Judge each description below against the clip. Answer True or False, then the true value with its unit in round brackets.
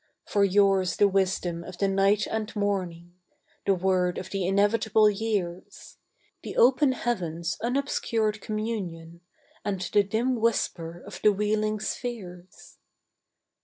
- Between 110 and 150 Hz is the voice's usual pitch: False (200 Hz)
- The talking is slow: True (125 wpm)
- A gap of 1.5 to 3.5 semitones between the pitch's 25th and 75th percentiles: True (3.1 semitones)